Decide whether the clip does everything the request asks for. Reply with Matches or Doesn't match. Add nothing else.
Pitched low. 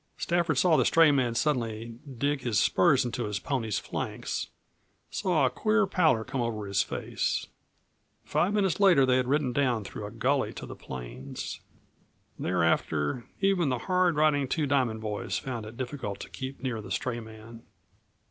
Matches